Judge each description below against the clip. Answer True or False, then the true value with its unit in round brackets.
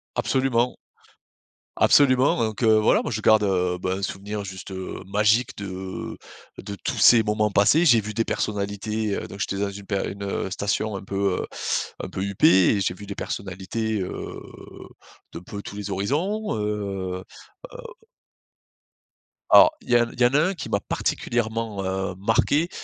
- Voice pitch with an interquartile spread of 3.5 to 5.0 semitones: False (2.7 semitones)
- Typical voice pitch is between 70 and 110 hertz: True (100 Hz)